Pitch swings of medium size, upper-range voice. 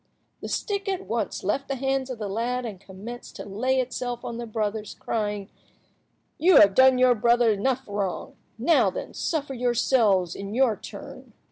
Yes: average, 4.0 semitones; high, 240 Hz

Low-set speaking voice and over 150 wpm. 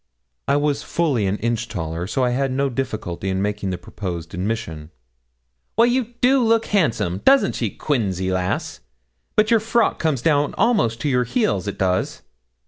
Yes: low, 120 Hz; average, 170 wpm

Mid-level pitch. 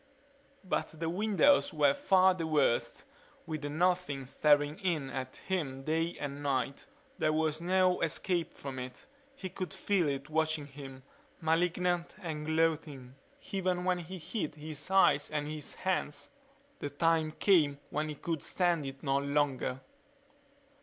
Yes: medium, 155 Hz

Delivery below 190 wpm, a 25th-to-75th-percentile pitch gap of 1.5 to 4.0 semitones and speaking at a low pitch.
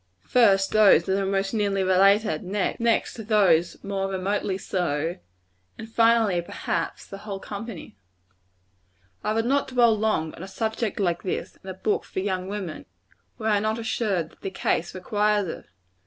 No: average, 155 wpm; narrow, 2.6 semitones; high, 200 Hz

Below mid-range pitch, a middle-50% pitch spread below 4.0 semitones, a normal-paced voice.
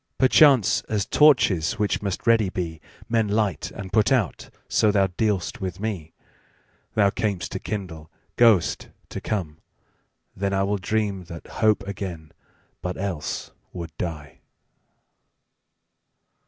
No: low, 100 Hz; average, 3.6 semitones; slow, 115 wpm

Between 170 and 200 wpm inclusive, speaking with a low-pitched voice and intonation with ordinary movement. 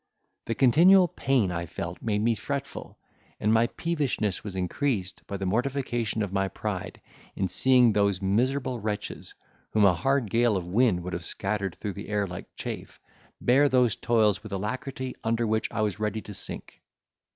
Yes: average, 175 wpm; low, 110 Hz; average, 4.3 semitones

